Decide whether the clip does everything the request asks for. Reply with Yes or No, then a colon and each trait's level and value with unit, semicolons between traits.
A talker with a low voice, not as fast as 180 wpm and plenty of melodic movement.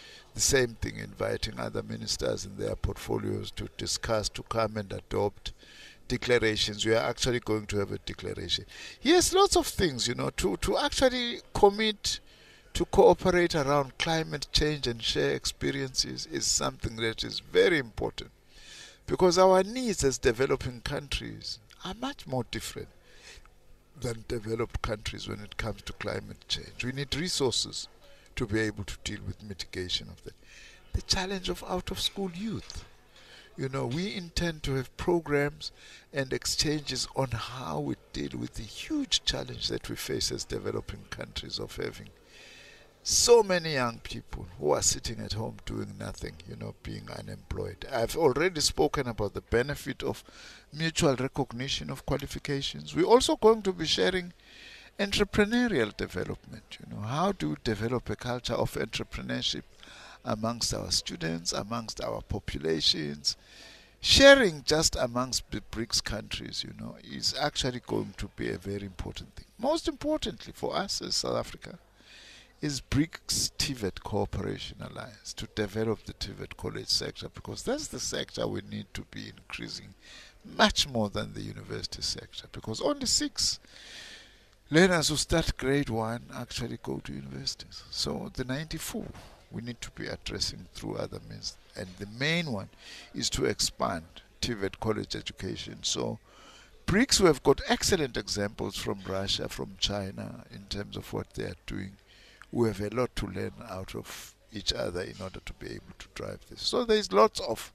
Yes: low, 115 Hz; average, 160 wpm; wide, 6.8 semitones